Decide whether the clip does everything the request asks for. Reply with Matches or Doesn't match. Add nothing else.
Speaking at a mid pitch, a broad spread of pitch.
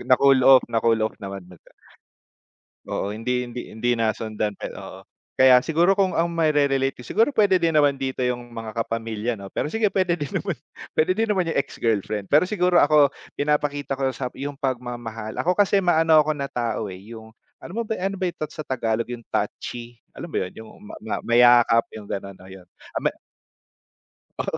Doesn't match